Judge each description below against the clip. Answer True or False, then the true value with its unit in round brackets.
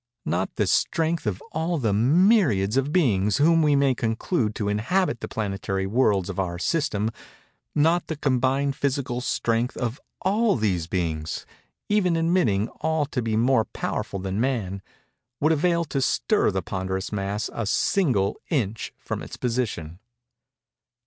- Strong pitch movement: True (7.6 semitones)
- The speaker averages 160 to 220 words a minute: False (140 wpm)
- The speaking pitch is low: True (120 Hz)